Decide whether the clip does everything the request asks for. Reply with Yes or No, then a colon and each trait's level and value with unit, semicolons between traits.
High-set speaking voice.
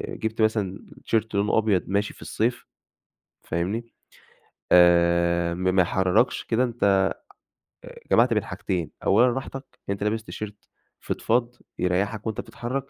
No: low, 105 Hz